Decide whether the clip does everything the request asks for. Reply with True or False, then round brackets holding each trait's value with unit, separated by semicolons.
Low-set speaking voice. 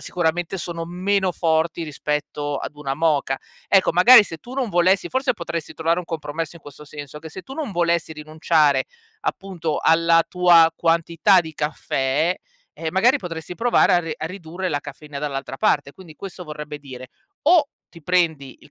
False (165 Hz)